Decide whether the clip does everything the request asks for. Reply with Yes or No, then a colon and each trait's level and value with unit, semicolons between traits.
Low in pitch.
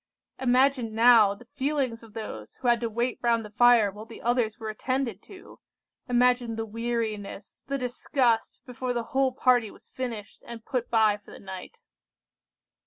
No: high, 235 Hz